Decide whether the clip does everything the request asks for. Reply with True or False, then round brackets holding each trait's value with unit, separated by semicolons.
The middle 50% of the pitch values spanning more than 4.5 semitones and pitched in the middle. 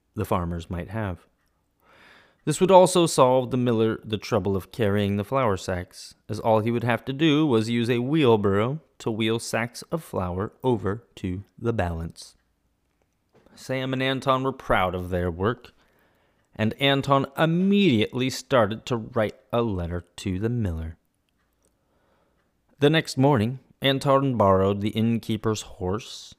False (5.4 semitones; 115 Hz)